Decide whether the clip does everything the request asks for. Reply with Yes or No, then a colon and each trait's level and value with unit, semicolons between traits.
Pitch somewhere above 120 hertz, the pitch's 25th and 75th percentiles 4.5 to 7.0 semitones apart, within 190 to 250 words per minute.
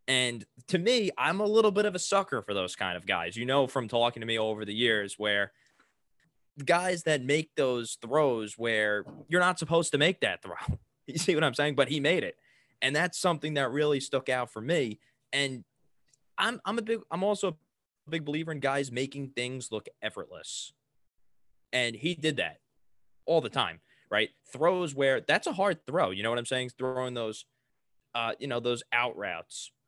Yes: low, 135 Hz; wide, 5.4 semitones; average, 200 wpm